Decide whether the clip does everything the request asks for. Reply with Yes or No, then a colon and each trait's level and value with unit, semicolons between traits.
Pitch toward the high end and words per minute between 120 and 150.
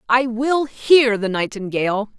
Yes: high, 235 Hz; slow, 135 wpm